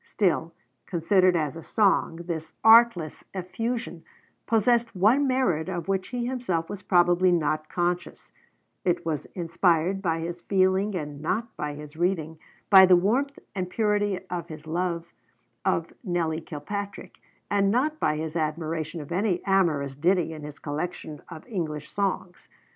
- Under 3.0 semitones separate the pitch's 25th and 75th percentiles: No, average, 3.7 semitones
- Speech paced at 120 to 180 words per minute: Yes, average, 150 wpm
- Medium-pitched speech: Yes, medium, 175 Hz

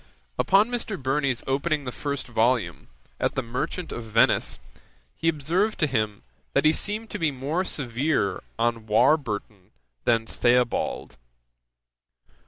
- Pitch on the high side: No, low, 135 Hz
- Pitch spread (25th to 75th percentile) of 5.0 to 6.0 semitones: Yes, wide, 5.5 semitones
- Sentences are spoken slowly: Yes, slow, 130 wpm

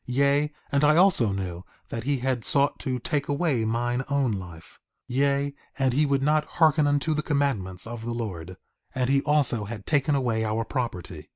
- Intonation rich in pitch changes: No, average, 4.3 semitones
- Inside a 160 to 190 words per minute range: Yes, average, 185 wpm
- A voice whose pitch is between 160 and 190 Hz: No, low, 130 Hz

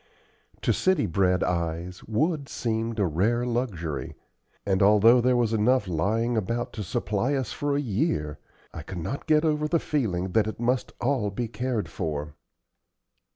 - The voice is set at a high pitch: No, low, 110 Hz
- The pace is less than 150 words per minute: No, average, 160 wpm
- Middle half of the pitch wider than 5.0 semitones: Yes, wide, 5.6 semitones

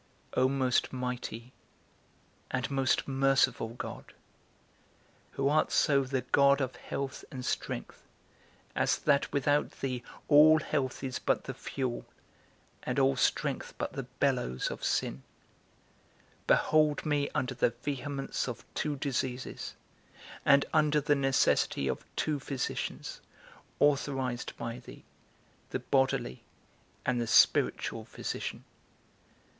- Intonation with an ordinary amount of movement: No, narrow, 2.1 semitones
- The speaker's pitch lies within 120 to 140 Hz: Yes, low, 135 Hz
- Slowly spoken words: Yes, slow, 120 wpm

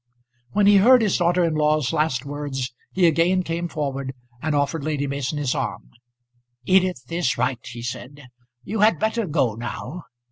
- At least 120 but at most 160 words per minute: No, average, 170 wpm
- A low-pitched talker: No, medium, 150 Hz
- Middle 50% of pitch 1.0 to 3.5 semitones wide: No, average, 4.8 semitones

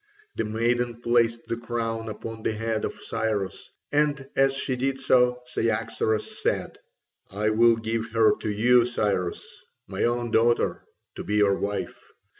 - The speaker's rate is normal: Yes, average, 150 wpm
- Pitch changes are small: Yes, narrow, 1.9 semitones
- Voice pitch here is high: No, low, 115 Hz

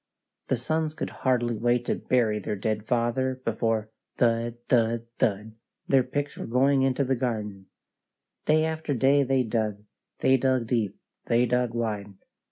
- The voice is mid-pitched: No, low, 120 Hz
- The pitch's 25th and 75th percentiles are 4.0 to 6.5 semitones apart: No, average, 2.9 semitones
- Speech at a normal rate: Yes, average, 155 wpm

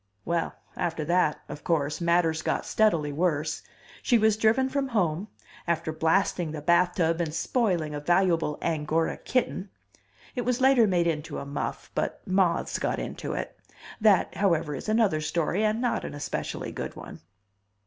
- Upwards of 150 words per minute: Yes, average, 160 wpm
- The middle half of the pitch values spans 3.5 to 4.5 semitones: No, average, 5.1 semitones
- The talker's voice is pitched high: No, medium, 170 Hz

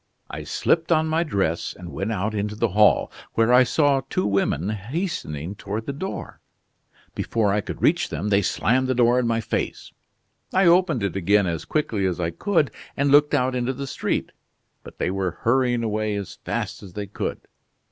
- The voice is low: Yes, low, 110 Hz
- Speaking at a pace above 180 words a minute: Yes, average, 190 wpm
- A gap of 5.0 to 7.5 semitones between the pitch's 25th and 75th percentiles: Yes, wide, 5.6 semitones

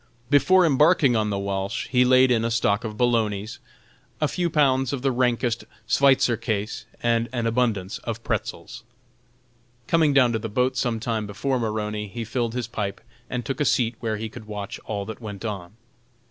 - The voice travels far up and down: No, average, 3.2 semitones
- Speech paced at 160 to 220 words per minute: Yes, average, 185 wpm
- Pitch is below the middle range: Yes, low, 115 Hz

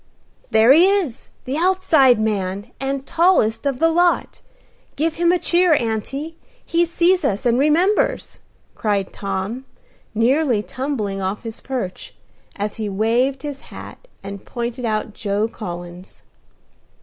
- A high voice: Yes, very high, 250 Hz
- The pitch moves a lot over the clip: Yes, wide, 7.3 semitones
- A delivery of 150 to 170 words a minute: No, slow, 135 wpm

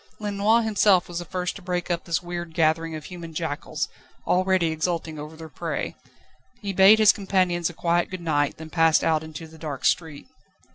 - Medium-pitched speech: Yes, medium, 170 Hz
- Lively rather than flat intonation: No, narrow, 2.6 semitones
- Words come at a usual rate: Yes, average, 190 wpm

